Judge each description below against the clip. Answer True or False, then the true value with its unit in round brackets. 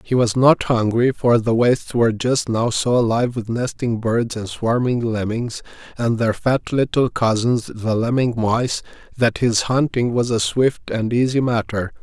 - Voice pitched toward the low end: True (120 Hz)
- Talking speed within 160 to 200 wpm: True (175 wpm)